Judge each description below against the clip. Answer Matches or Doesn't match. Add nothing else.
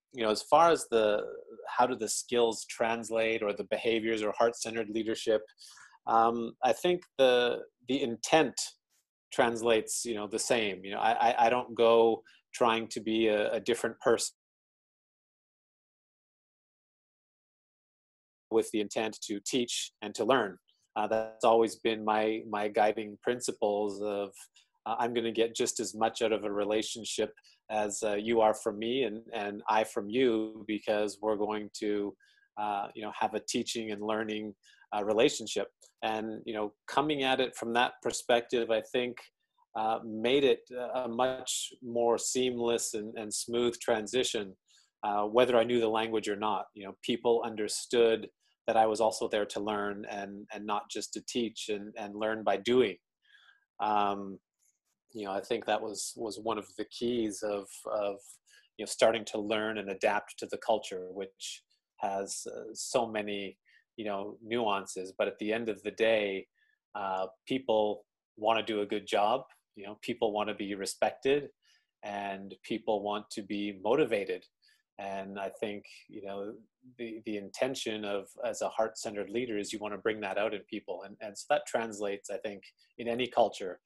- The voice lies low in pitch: Matches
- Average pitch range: Doesn't match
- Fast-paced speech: Doesn't match